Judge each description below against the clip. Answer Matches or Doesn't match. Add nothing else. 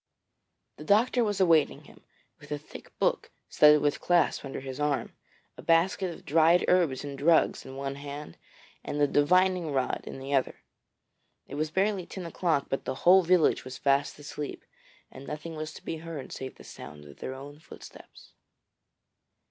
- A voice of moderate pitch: Matches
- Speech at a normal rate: Matches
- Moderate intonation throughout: Matches